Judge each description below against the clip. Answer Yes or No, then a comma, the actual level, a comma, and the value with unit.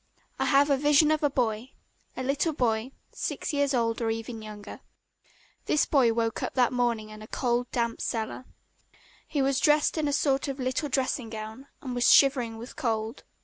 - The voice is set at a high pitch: Yes, very high, 250 Hz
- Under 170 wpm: No, average, 190 wpm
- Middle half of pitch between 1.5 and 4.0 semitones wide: Yes, average, 3.5 semitones